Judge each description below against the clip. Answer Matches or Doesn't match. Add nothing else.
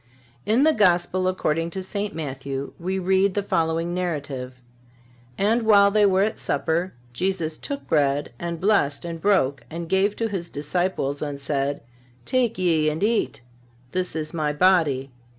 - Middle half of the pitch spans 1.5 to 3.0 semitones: Doesn't match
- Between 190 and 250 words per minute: Doesn't match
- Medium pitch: Matches